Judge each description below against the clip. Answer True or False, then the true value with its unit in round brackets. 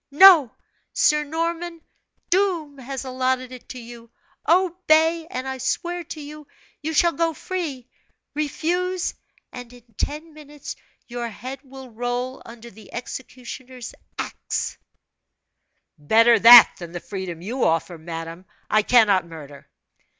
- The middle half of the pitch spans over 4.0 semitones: True (5.2 semitones)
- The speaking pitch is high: True (260 Hz)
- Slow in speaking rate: True (130 wpm)